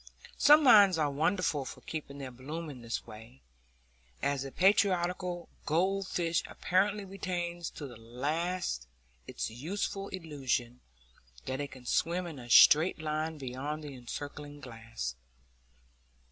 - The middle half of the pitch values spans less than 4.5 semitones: No, wide, 5.6 semitones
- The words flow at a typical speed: No, slow, 130 wpm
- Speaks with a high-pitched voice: No, medium, 150 Hz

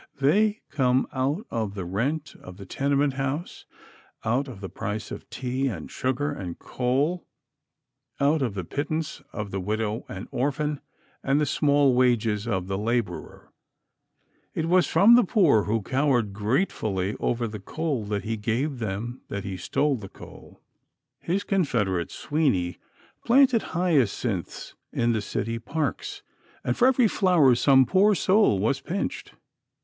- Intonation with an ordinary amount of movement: No, wide, 6.4 semitones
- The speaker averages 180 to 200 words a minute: No, average, 150 wpm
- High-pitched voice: No, low, 130 Hz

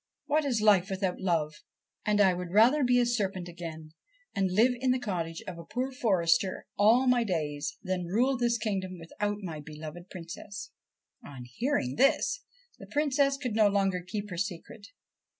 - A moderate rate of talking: Yes, average, 170 wpm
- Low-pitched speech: No, high, 195 Hz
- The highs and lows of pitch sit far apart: Yes, wide, 5.7 semitones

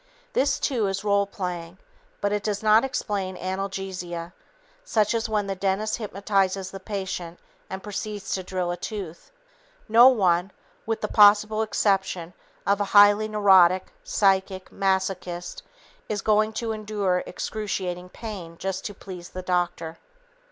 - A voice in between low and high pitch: No, high, 195 Hz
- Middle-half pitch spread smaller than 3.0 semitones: Yes, narrow, 2.4 semitones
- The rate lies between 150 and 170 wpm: No, average, 140 wpm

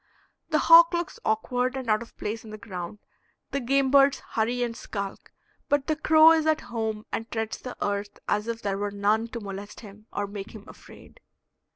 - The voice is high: Yes, high, 225 Hz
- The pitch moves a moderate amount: Yes, average, 4.8 semitones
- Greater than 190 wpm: Yes, average, 200 wpm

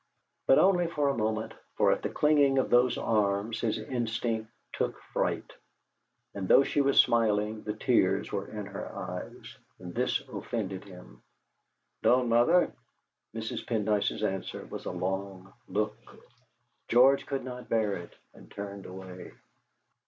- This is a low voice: Yes, low, 110 Hz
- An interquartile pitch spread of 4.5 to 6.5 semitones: No, average, 3.9 semitones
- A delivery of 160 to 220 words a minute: No, average, 145 wpm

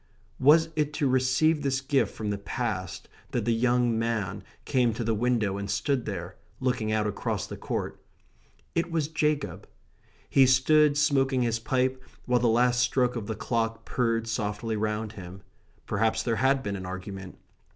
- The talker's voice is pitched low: Yes, low, 120 Hz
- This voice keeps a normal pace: Yes, average, 170 wpm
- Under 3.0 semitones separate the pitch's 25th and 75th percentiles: No, average, 3.6 semitones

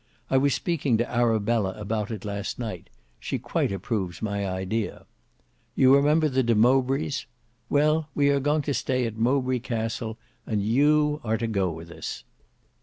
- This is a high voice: No, low, 120 Hz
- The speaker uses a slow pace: No, average, 165 wpm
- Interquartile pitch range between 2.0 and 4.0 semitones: No, average, 4.7 semitones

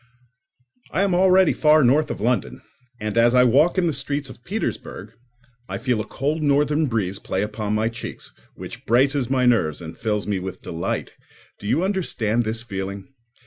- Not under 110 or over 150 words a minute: No, average, 180 wpm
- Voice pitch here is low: Yes, low, 125 Hz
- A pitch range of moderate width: No, wide, 5.8 semitones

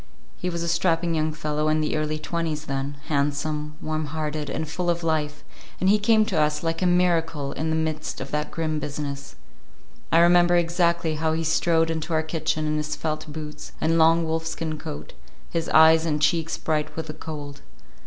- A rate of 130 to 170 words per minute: No, average, 195 wpm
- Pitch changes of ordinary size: No, narrow, 1.5 semitones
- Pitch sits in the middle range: Yes, medium, 160 Hz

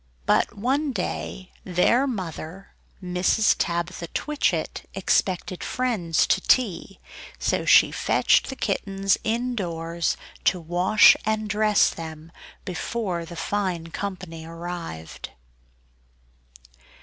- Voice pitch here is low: No, medium, 185 Hz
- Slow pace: Yes, slow, 100 wpm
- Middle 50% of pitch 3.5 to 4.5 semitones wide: Yes, average, 4.1 semitones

